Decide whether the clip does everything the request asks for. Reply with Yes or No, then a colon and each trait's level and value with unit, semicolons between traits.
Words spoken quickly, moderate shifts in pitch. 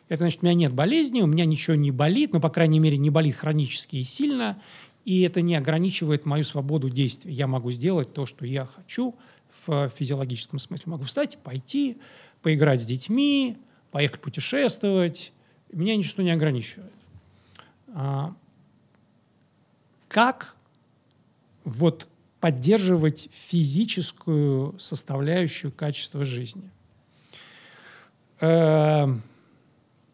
No: average, 115 wpm; average, 4.3 semitones